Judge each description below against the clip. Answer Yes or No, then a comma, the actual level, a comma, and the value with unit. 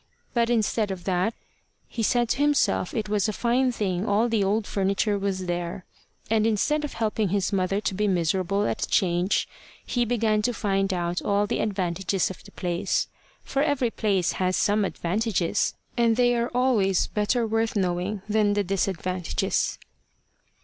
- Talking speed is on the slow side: No, average, 170 wpm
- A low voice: No, high, 205 Hz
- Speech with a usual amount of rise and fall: Yes, average, 3.2 semitones